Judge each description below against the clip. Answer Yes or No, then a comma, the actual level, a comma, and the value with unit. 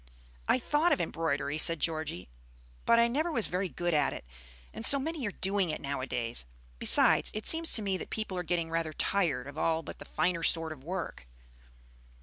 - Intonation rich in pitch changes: Yes, wide, 5.7 semitones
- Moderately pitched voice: Yes, medium, 170 Hz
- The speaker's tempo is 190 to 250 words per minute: Yes, average, 195 wpm